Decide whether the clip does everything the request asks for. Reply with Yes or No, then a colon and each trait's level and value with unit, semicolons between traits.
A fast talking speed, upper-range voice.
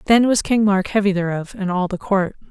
Yes: fast, 240 wpm; high, 195 Hz